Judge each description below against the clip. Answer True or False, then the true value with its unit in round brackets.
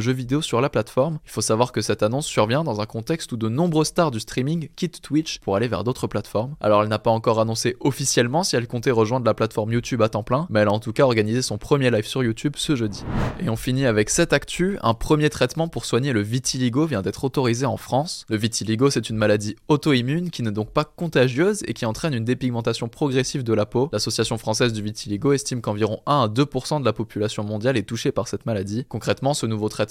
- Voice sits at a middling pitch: False (120 Hz)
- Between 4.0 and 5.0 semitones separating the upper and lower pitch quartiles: True (4.3 semitones)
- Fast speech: True (240 wpm)